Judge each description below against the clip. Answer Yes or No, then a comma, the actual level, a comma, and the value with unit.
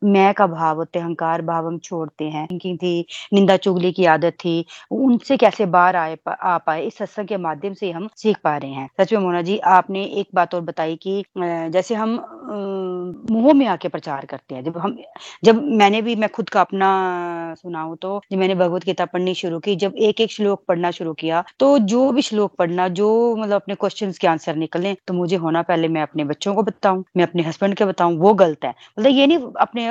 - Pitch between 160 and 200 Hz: Yes, medium, 185 Hz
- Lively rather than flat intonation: No, average, 3.5 semitones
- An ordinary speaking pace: No, fast, 215 wpm